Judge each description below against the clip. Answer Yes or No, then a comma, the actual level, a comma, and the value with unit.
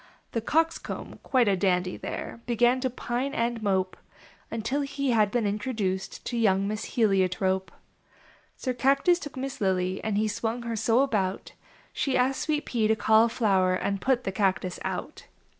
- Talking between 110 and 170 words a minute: Yes, average, 160 wpm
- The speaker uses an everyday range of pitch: Yes, average, 4.6 semitones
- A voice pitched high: Yes, high, 225 Hz